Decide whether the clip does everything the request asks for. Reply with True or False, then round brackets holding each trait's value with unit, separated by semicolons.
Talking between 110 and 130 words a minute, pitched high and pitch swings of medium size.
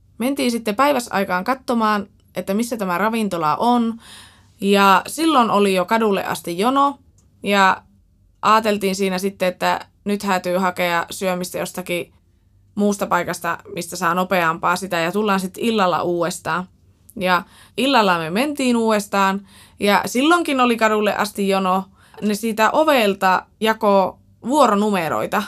True (125 wpm; 195 Hz; 3.7 semitones)